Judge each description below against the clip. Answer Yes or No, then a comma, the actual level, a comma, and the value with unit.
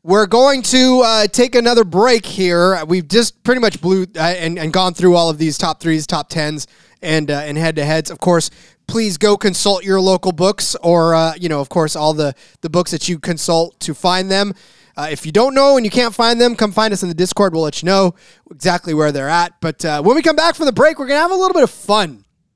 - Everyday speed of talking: No, fast, 250 wpm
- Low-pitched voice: No, medium, 180 Hz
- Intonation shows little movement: No, average, 5.1 semitones